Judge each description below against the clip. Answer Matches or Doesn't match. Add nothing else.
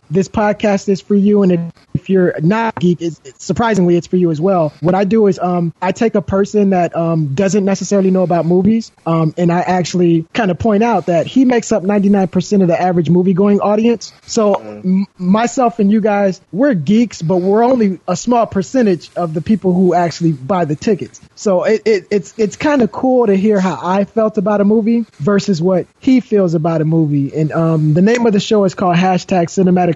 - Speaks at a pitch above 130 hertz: Matches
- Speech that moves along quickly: Matches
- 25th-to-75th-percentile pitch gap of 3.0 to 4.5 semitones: Matches